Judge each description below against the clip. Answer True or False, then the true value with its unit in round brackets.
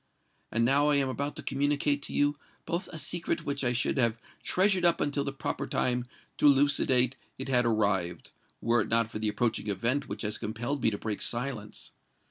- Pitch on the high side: False (130 Hz)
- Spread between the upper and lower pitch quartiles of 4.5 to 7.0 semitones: False (4.1 semitones)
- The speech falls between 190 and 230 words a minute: True (195 wpm)